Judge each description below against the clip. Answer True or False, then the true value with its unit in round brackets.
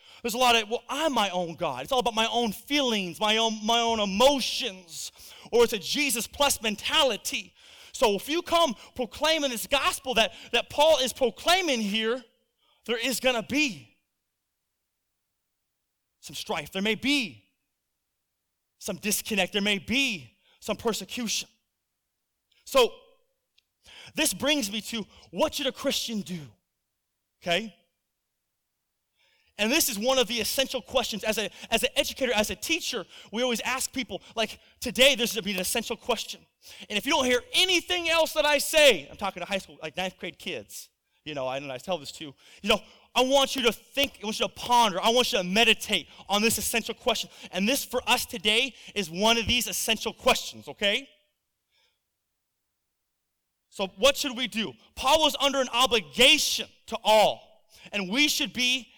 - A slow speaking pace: False (175 wpm)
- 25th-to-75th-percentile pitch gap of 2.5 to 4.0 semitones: False (4.8 semitones)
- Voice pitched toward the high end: True (230 Hz)